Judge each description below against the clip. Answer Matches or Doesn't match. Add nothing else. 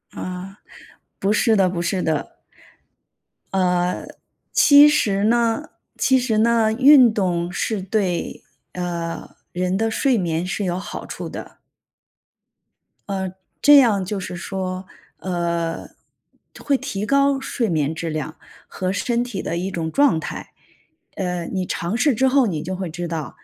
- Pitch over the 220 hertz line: Doesn't match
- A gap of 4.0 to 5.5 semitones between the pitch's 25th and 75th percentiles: Matches